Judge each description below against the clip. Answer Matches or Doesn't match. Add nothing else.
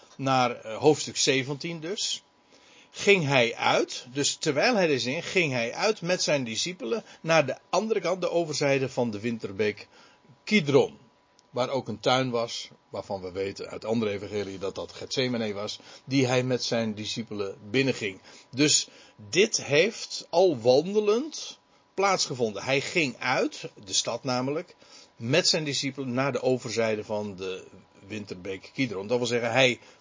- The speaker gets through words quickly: Doesn't match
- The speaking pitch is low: Matches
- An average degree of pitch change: Matches